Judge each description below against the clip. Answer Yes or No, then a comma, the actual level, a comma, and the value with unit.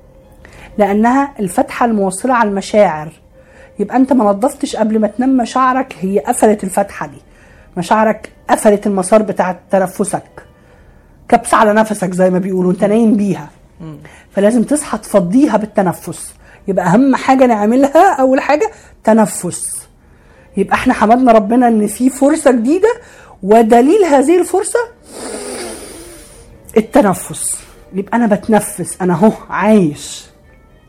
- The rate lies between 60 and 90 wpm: No, average, 115 wpm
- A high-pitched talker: Yes, high, 215 Hz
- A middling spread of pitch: Yes, average, 4.7 semitones